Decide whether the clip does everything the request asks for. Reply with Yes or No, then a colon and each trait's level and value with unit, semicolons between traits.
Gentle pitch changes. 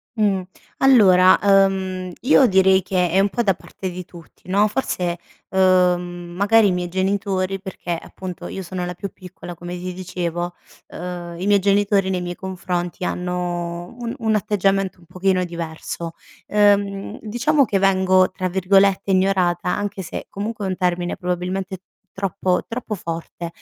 Yes: narrow, 1.8 semitones